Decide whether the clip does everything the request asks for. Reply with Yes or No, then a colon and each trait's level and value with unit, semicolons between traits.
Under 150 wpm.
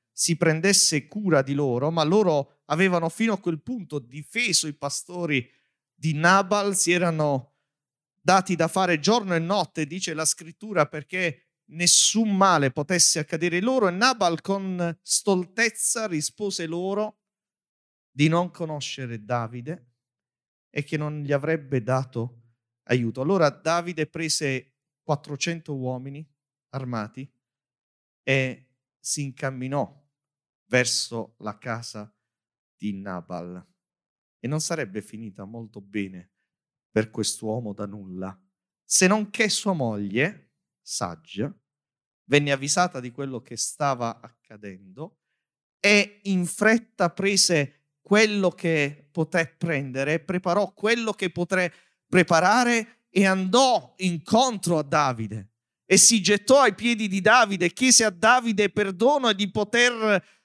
Yes: average, 120 wpm